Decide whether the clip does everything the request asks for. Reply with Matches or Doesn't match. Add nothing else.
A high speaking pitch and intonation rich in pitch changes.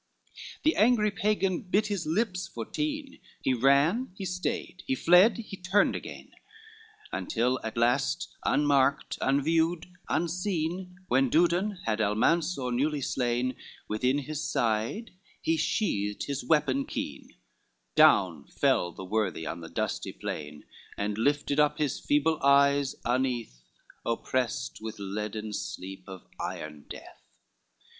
Doesn't match